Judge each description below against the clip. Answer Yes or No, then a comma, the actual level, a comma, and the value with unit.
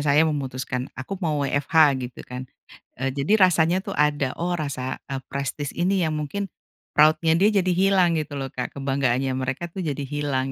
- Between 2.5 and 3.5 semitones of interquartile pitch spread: No, average, 4.3 semitones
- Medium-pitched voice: Yes, medium, 145 Hz